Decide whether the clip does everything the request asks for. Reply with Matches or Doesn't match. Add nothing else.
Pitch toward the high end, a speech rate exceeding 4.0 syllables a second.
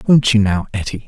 Doesn't match